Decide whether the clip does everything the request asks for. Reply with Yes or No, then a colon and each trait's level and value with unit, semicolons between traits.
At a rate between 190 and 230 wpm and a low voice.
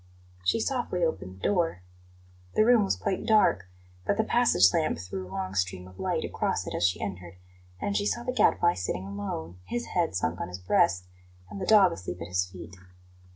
Yes: average, 200 wpm; very low, 95 Hz